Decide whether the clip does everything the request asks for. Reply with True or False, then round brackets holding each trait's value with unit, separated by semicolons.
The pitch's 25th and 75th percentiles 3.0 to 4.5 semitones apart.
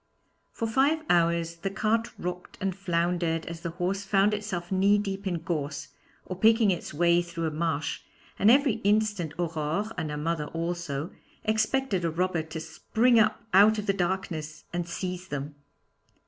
True (3.7 semitones)